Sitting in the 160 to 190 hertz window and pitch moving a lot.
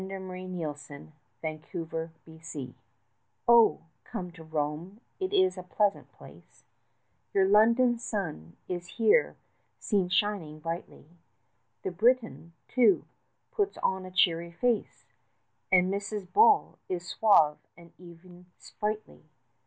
No: medium, 185 Hz; average, 4.6 semitones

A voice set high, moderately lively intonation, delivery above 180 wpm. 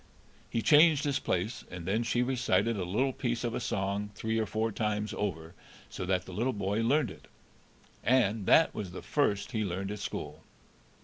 No: low, 110 Hz; average, 3.9 semitones; average, 190 wpm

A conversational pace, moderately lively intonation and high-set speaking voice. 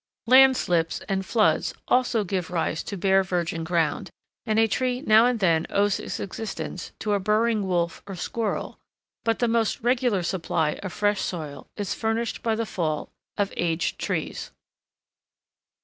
Yes: average, 160 wpm; average, 4.4 semitones; high, 200 Hz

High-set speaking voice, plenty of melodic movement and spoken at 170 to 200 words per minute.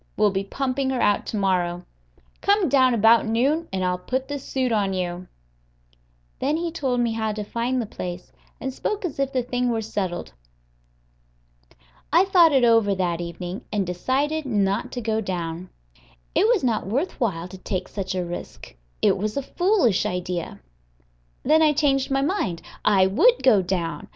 Yes: high, 225 Hz; wide, 6.4 semitones; average, 175 wpm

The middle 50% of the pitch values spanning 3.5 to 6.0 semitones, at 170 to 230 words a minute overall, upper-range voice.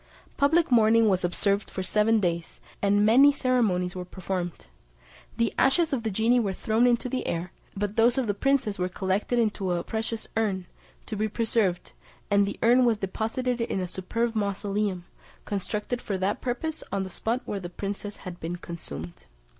Yes: average, 3.8 semitones; average, 180 wpm; high, 210 Hz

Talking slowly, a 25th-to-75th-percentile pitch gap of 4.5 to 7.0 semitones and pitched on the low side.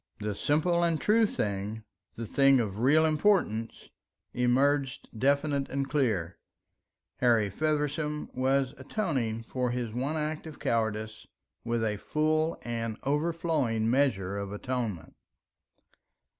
Yes: slow, 120 wpm; average, 5.3 semitones; low, 130 Hz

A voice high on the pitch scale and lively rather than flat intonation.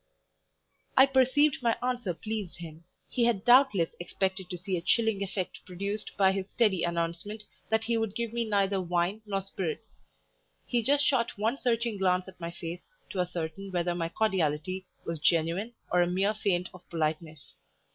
No: high, 195 Hz; average, 4.3 semitones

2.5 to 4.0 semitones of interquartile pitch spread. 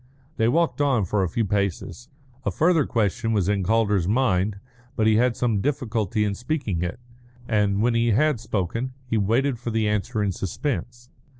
Yes: average, 3.4 semitones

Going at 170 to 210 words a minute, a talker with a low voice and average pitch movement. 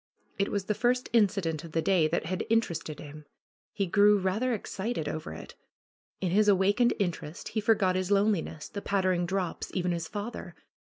No: average, 180 wpm; high, 195 Hz; average, 3.4 semitones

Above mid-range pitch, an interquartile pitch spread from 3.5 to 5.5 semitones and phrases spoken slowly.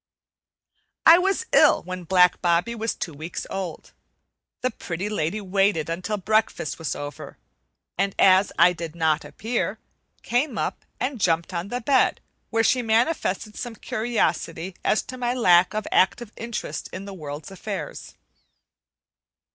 No: high, 195 Hz; average, 5.1 semitones; average, 145 wpm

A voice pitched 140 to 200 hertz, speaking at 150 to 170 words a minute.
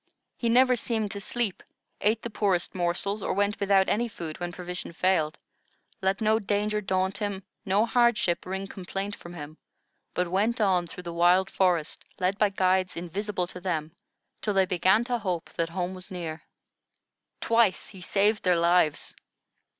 Yes: high, 190 Hz; average, 165 wpm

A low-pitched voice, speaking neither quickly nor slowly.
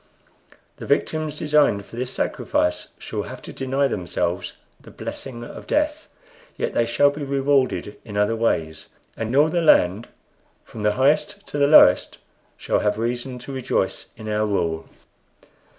Yes: low, 125 Hz; average, 155 wpm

